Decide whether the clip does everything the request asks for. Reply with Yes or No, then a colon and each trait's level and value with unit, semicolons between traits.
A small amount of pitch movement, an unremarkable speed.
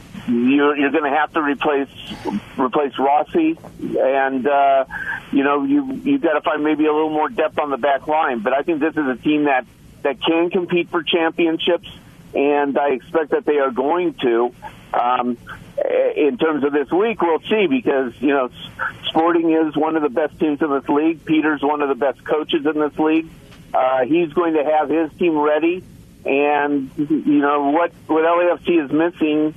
No: average, 3.0 semitones; average, 190 wpm